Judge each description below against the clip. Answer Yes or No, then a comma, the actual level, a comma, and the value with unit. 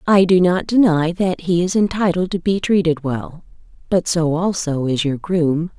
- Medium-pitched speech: Yes, medium, 175 Hz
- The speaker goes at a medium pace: Yes, average, 175 wpm